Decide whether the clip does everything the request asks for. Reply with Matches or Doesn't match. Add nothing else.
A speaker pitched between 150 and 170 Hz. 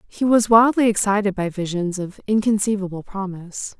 Doesn't match